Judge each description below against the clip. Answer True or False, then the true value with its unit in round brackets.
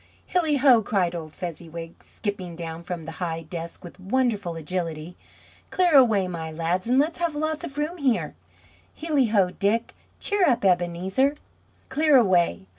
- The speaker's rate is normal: True (155 wpm)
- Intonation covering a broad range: True (8.0 semitones)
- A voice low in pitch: False (190 Hz)